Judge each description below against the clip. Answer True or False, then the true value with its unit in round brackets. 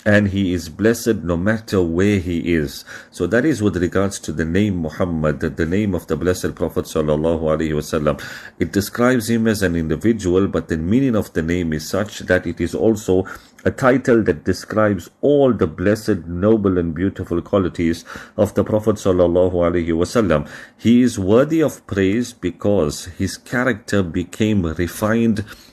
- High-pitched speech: False (95 Hz)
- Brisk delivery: False (170 wpm)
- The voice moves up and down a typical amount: True (4.0 semitones)